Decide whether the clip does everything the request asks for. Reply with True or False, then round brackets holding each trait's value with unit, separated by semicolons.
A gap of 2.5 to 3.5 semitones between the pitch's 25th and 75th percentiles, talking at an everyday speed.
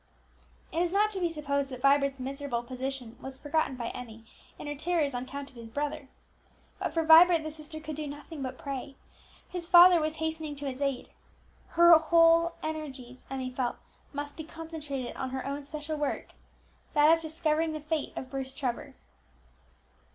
True (3.2 semitones; 180 wpm)